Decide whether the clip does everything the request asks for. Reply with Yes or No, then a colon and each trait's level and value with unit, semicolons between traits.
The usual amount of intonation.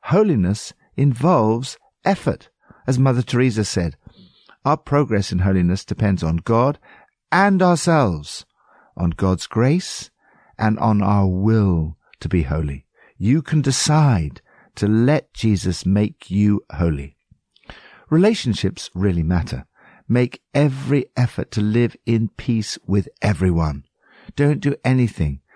No: wide, 6.4 semitones